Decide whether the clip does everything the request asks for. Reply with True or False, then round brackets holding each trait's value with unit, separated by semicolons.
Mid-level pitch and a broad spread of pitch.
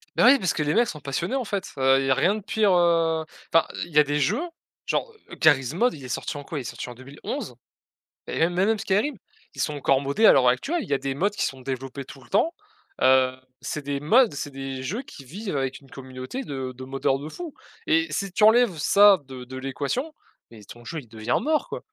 True (145 Hz; 7.3 semitones)